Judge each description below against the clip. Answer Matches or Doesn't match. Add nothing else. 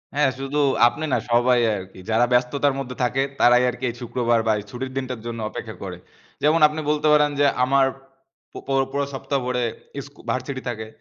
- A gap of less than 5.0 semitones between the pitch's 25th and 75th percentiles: Matches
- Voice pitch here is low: Matches